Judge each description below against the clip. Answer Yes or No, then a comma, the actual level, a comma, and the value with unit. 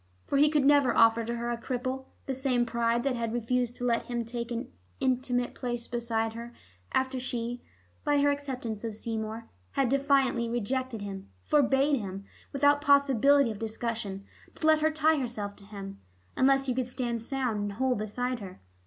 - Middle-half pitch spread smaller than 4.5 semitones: Yes, average, 2.8 semitones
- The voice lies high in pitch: Yes, high, 245 Hz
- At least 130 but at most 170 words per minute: No, average, 180 wpm